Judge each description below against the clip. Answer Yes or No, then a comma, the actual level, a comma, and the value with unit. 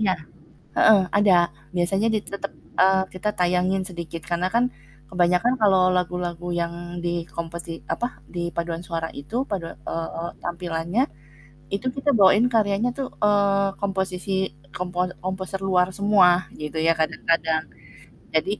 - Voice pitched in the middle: Yes, medium, 180 Hz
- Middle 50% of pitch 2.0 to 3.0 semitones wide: Yes, average, 2.7 semitones